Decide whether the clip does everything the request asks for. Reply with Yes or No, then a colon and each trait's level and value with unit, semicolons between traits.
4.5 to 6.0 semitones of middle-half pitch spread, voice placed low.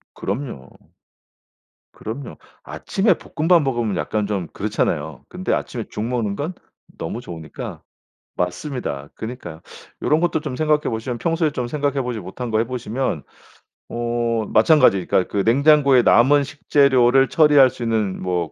Yes: wide, 5.5 semitones; low, 120 Hz